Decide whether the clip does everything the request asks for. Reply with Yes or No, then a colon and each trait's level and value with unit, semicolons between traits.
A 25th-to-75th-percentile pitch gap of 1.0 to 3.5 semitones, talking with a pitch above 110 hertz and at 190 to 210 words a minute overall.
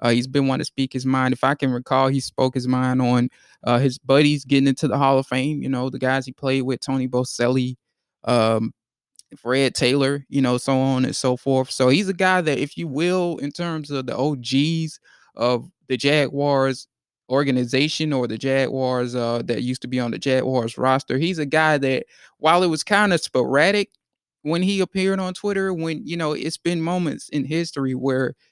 Yes: average, 3.1 semitones; low, 135 Hz; fast, 205 wpm